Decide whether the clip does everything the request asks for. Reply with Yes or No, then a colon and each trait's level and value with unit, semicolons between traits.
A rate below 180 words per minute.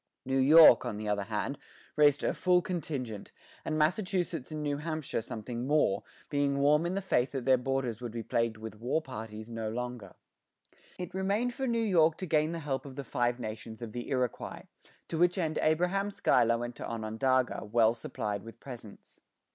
No: average, 185 wpm